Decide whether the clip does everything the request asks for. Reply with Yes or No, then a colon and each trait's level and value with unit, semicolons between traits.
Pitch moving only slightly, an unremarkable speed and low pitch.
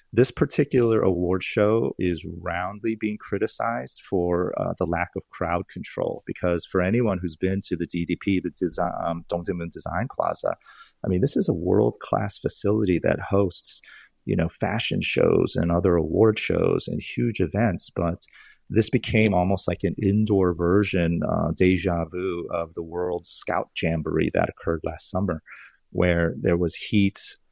No: average, 3.4 semitones; average, 160 wpm; very low, 90 Hz